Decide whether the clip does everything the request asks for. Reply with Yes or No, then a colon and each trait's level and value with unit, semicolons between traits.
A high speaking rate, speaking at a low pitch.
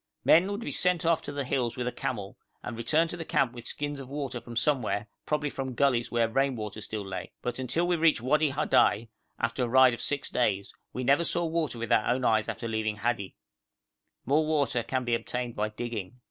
Yes: fast, 220 wpm; low, 125 Hz